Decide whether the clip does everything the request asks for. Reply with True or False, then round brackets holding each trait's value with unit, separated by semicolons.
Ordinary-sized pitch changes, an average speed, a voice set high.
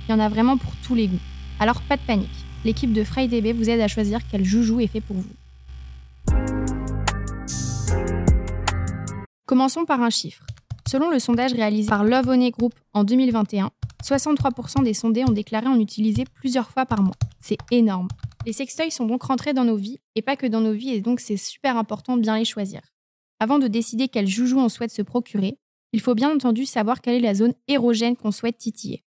True (4.1 semitones; 200 wpm; 225 Hz)